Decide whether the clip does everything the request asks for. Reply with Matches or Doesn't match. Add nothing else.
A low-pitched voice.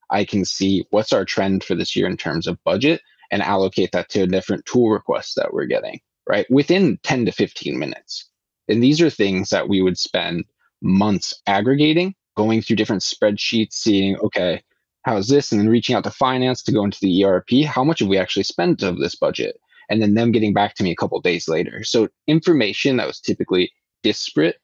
Matches